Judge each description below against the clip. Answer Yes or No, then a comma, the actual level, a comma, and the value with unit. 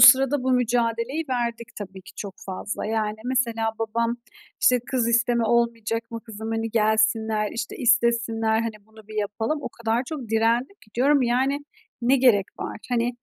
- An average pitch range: No, narrow, 1.8 semitones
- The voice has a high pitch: Yes, high, 230 Hz